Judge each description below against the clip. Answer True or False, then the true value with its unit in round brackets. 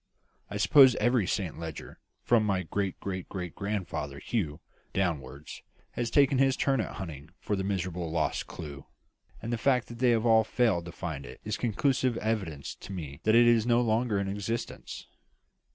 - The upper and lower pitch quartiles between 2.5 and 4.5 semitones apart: False (5.5 semitones)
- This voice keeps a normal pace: True (175 wpm)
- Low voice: True (100 Hz)